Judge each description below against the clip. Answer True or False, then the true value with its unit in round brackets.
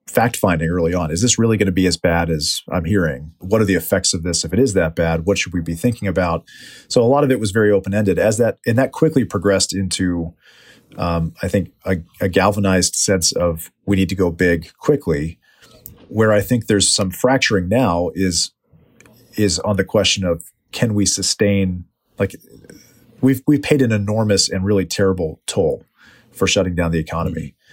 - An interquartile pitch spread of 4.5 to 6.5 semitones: False (3.4 semitones)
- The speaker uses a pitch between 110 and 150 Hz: False (95 Hz)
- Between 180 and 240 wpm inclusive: True (200 wpm)